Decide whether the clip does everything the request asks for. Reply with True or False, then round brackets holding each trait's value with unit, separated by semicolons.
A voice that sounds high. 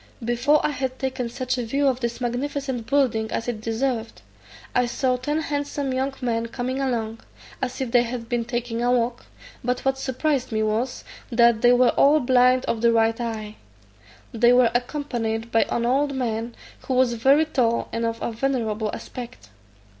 True (245 Hz)